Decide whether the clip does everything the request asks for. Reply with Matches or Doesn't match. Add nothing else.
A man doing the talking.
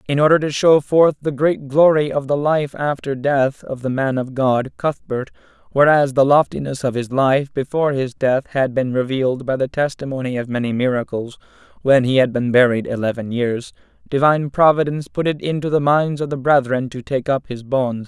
Matches